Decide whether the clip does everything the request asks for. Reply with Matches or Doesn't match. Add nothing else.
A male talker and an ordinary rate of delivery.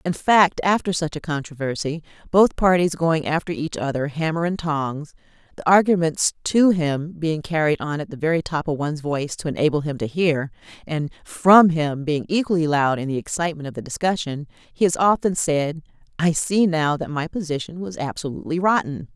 Doesn't match